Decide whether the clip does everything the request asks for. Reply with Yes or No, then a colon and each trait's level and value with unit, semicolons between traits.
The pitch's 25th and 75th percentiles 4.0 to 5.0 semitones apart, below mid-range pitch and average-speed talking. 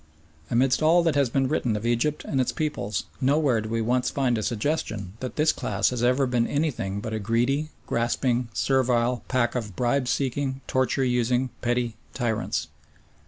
No: narrow, 2.5 semitones; low, 125 Hz; average, 170 wpm